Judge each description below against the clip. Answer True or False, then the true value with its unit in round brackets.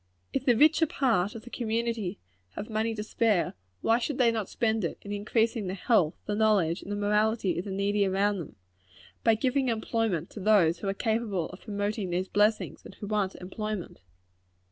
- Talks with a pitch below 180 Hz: False (210 Hz)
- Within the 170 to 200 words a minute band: True (190 wpm)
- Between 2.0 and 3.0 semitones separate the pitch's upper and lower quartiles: True (2.6 semitones)